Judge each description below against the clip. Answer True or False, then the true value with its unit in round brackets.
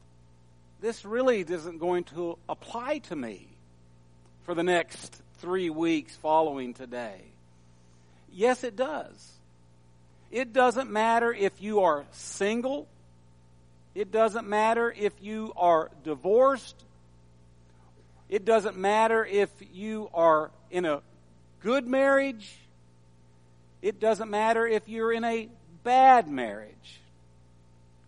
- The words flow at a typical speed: False (110 wpm)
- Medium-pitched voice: True (165 Hz)